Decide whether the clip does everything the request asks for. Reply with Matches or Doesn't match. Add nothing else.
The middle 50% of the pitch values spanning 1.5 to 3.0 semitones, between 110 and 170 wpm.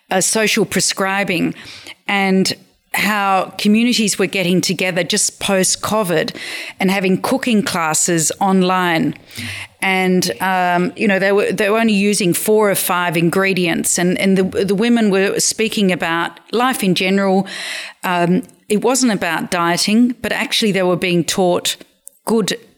Matches